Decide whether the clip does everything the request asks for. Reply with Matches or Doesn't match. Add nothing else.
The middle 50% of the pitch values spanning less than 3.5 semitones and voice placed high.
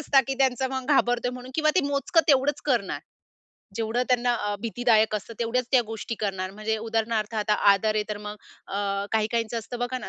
Matches